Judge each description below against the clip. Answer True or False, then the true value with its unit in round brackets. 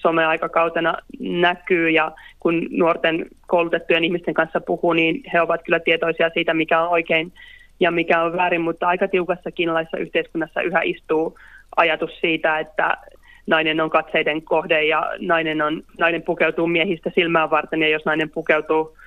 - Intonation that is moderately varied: False (1.2 semitones)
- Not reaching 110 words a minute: False (150 wpm)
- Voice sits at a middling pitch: True (165 Hz)